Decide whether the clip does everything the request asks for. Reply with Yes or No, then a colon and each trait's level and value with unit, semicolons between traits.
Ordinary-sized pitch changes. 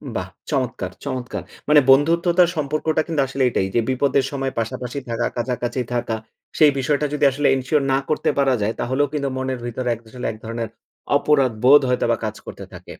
Yes: average, 3.1 semitones